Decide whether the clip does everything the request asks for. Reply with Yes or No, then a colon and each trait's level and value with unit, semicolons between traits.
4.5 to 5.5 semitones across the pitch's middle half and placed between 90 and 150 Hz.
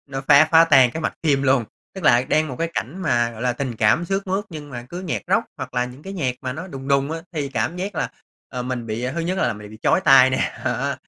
Yes: average, 5.0 semitones; low, 135 Hz